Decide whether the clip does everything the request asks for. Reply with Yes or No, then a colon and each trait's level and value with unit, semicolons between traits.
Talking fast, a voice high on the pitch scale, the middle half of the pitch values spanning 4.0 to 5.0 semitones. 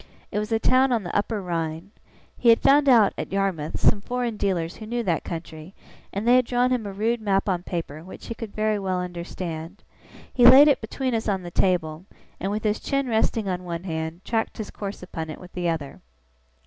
Yes: fast, 220 wpm; high, 200 Hz; average, 4.7 semitones